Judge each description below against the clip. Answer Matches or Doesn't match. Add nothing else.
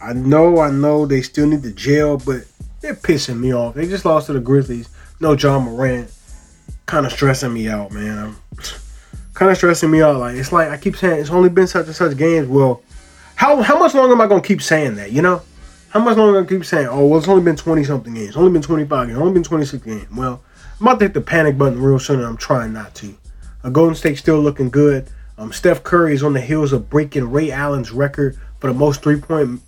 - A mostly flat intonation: Doesn't match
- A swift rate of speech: Matches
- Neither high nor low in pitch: Matches